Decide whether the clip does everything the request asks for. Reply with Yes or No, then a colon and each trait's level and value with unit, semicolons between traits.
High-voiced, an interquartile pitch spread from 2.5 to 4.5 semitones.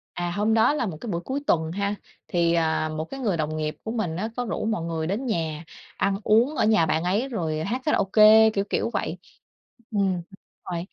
No: high, 195 Hz; average, 5.1 semitones